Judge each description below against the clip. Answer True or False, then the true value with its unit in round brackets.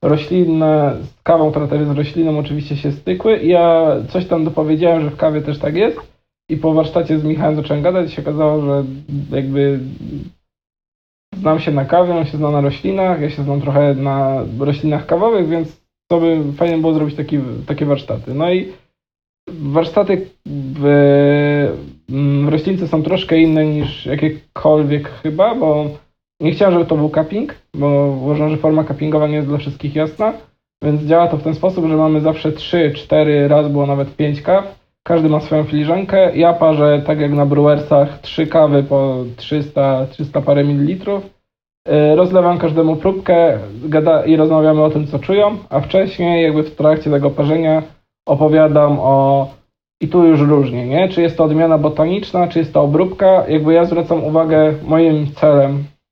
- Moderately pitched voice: True (155 Hz)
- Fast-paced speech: True (165 wpm)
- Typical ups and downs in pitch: False (2.3 semitones)